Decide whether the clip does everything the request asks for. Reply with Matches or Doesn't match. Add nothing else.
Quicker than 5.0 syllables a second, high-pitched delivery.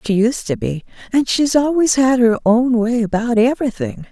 Doesn't match